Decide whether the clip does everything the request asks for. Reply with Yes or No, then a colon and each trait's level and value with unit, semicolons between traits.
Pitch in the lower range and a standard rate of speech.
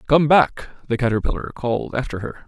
Yes: low, 130 Hz; average, 170 wpm